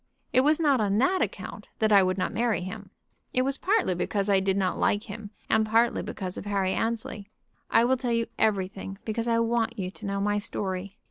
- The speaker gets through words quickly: Yes, fast, 215 wpm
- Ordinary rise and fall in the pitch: Yes, average, 3.1 semitones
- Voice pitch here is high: Yes, high, 210 Hz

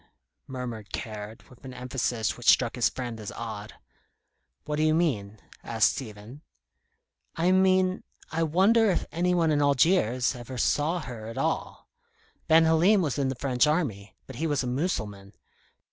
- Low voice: Yes, low, 130 Hz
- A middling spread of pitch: No, wide, 6.0 semitones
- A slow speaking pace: No, average, 160 wpm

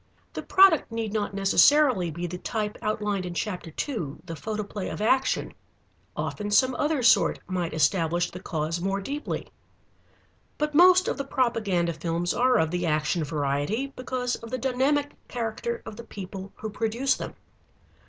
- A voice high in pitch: Yes, high, 210 Hz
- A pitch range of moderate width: No, wide, 6.3 semitones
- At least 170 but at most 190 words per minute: No, average, 160 wpm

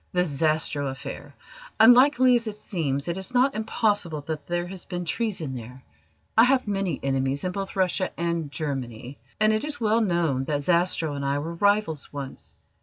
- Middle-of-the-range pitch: Yes, medium, 170 Hz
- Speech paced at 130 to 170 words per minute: No, average, 180 wpm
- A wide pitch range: Yes, wide, 6.7 semitones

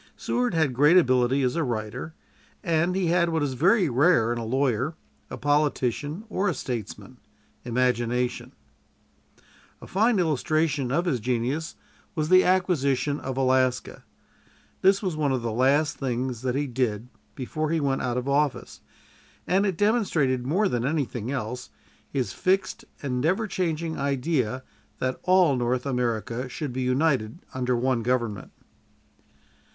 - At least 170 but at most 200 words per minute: No, average, 145 wpm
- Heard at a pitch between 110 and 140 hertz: Yes, low, 135 Hz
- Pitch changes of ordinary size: Yes, average, 4.6 semitones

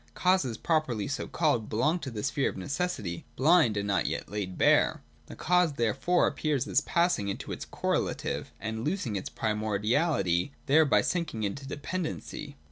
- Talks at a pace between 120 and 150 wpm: No, average, 160 wpm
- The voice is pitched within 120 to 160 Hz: Yes, low, 135 Hz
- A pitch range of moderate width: No, wide, 7.1 semitones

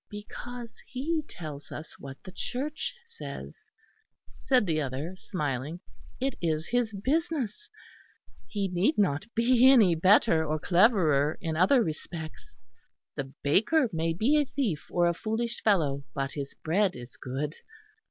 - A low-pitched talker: No, medium, 185 Hz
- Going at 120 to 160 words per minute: Yes, average, 140 wpm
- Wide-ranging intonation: Yes, wide, 7.7 semitones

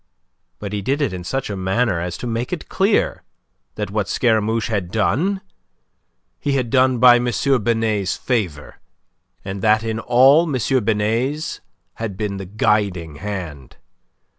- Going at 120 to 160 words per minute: Yes, average, 150 wpm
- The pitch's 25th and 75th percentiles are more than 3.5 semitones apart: Yes, average, 4.2 semitones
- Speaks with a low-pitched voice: Yes, low, 110 Hz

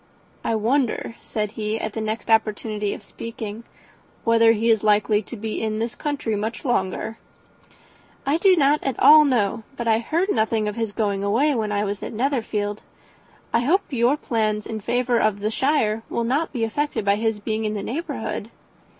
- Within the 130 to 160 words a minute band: No, average, 185 wpm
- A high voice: Yes, high, 225 Hz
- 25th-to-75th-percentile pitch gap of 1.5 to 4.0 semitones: Yes, narrow, 2.5 semitones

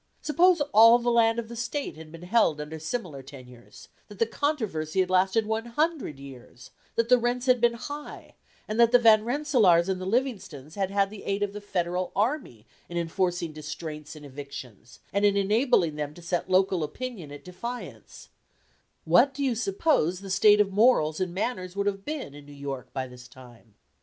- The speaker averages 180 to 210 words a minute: Yes, average, 190 wpm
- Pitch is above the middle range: Yes, high, 195 Hz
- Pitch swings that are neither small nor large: No, wide, 7.2 semitones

